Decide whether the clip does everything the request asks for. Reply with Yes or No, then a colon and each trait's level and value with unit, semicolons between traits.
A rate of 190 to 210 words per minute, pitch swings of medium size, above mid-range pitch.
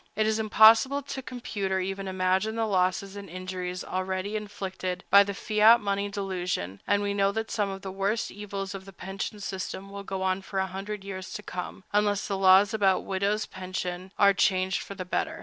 No: average, 200 wpm; narrow, 1.7 semitones; high, 195 Hz